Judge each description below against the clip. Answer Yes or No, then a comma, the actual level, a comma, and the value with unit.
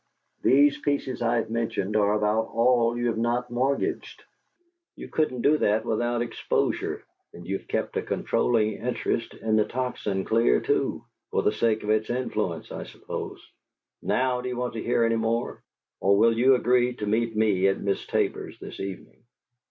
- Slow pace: No, average, 170 wpm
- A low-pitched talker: Yes, low, 115 Hz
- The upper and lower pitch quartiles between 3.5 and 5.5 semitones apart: No, narrow, 2.4 semitones